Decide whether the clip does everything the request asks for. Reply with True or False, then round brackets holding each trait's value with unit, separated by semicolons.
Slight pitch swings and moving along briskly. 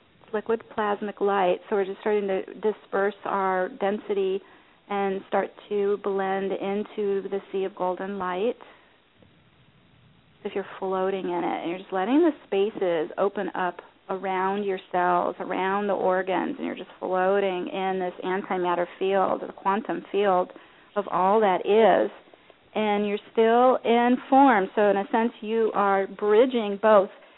False (1.9 semitones; 150 wpm)